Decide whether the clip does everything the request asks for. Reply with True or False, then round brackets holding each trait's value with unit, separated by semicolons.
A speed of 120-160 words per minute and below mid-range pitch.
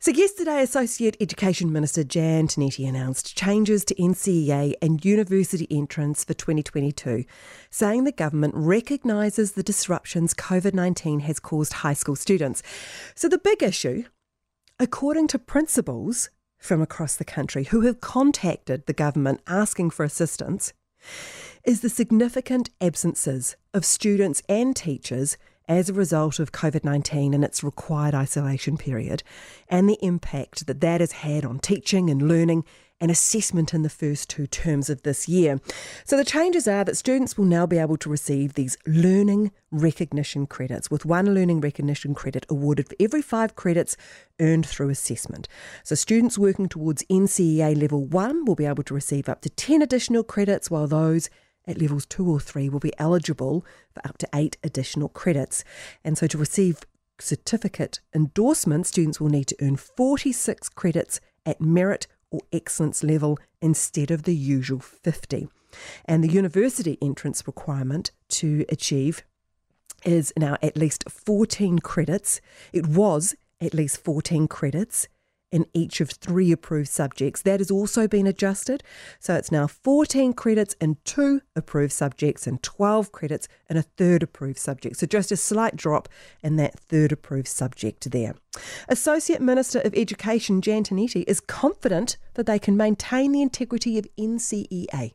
False (155 wpm; 165 Hz)